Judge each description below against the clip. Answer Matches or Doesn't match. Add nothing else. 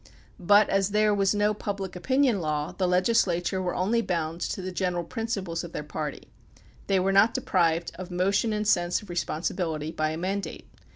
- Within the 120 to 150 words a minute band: Doesn't match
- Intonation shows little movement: Doesn't match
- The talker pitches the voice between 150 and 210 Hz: Matches